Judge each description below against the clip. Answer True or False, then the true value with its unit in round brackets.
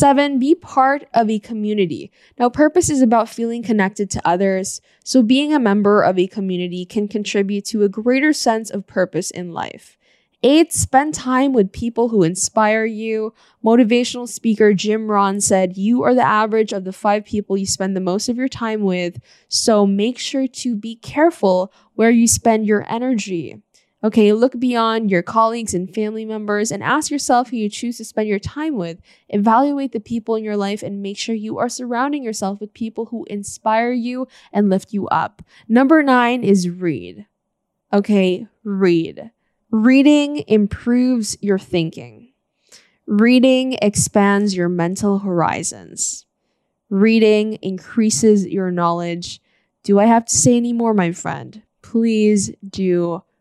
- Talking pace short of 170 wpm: True (160 wpm)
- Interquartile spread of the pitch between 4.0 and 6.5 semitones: False (3.4 semitones)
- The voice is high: True (215 Hz)